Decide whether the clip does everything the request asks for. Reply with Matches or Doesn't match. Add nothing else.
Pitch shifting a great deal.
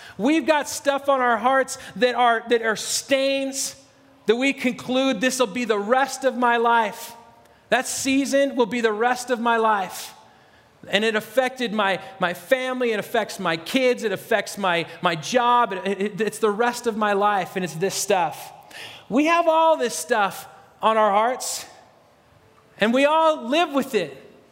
Doesn't match